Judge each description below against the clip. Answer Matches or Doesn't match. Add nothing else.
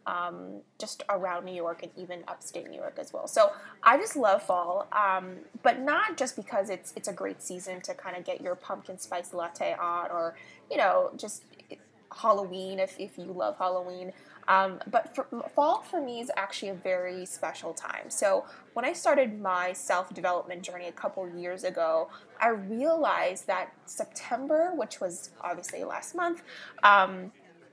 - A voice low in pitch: Doesn't match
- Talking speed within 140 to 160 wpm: Doesn't match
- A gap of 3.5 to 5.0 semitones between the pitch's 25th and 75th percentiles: Doesn't match